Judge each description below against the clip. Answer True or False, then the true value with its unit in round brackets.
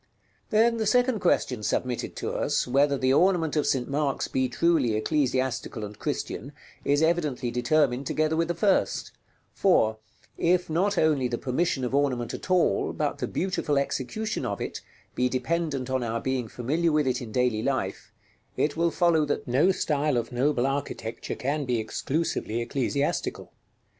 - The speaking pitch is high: False (140 Hz)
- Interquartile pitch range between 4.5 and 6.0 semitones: True (4.9 semitones)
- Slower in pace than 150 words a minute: False (170 wpm)